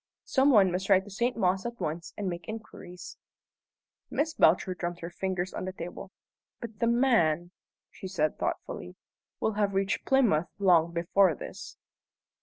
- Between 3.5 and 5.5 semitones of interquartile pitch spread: Yes, average, 3.8 semitones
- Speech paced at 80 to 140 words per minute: No, average, 160 wpm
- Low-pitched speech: No, high, 190 Hz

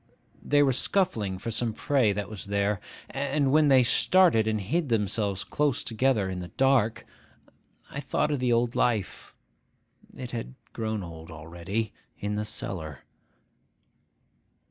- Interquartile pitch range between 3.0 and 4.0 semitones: No, average, 5.1 semitones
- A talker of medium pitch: No, low, 110 Hz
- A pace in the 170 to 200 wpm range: No, average, 145 wpm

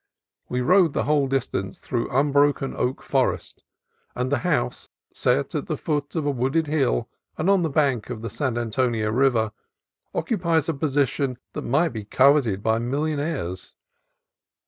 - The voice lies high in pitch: No, low, 135 Hz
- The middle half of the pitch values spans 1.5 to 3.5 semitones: No, average, 4.1 semitones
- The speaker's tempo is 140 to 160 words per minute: Yes, average, 155 wpm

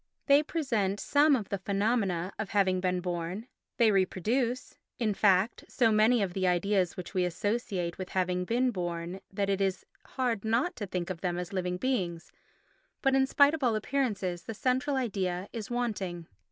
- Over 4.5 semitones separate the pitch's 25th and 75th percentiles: Yes, average, 4.9 semitones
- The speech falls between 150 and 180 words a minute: Yes, average, 170 wpm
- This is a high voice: Yes, high, 200 Hz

